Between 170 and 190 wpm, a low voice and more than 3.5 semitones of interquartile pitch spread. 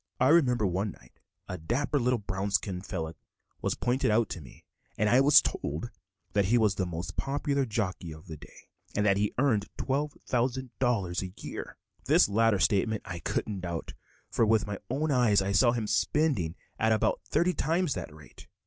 Yes: average, 185 wpm; low, 105 Hz; average, 5.3 semitones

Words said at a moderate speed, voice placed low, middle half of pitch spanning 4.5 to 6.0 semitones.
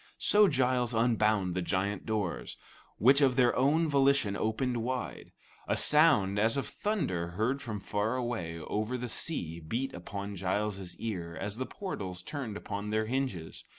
Yes: average, 155 wpm; low, 110 Hz; average, 4.8 semitones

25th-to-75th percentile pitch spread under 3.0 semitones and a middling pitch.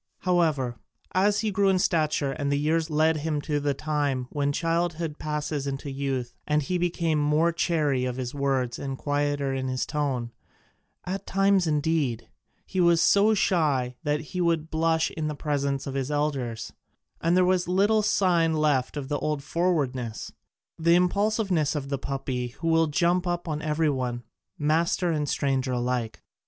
No: average, 3.7 semitones; medium, 150 Hz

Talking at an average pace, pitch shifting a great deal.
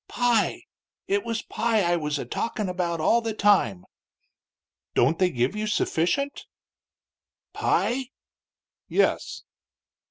No: slow, 115 wpm; wide, 5.7 semitones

